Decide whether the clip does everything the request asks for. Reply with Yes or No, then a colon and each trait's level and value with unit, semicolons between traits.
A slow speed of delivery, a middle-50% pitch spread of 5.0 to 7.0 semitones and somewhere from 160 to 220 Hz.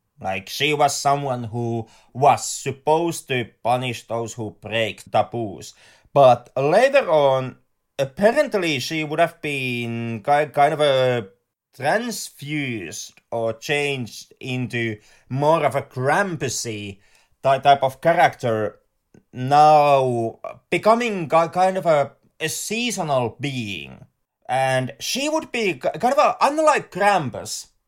No: slow, 110 wpm; average, 5.3 semitones; low, 135 Hz